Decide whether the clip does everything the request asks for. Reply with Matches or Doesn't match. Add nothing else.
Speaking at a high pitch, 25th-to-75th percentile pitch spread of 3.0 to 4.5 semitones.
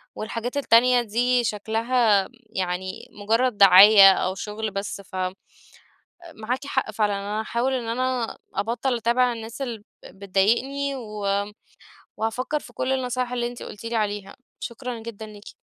Matches